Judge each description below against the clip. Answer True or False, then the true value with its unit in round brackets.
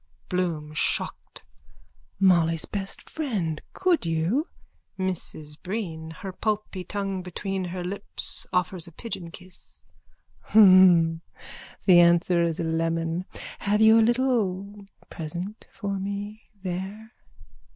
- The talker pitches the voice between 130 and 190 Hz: True (185 Hz)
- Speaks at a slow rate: True (110 wpm)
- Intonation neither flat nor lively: True (3.4 semitones)